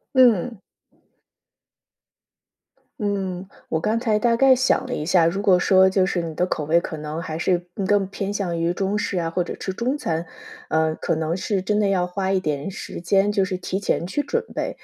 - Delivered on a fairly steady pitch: No, average, 3.3 semitones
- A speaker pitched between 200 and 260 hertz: No, high, 190 Hz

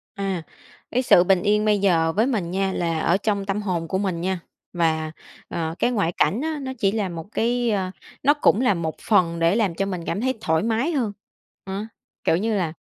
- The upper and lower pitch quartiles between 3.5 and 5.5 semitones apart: Yes, average, 4.4 semitones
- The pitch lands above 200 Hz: No, high, 195 Hz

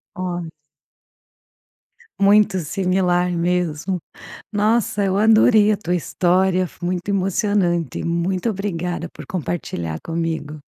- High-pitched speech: No, medium, 180 Hz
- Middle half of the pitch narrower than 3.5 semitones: Yes, average, 2.7 semitones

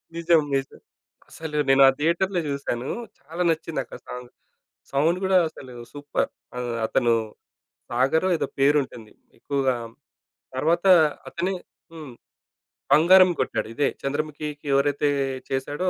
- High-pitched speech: No, medium, 145 Hz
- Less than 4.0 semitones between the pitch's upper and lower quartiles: Yes, average, 3.6 semitones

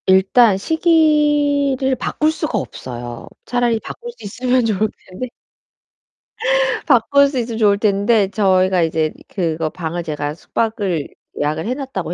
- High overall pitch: Yes, high, 215 Hz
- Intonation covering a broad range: Yes, wide, 6.5 semitones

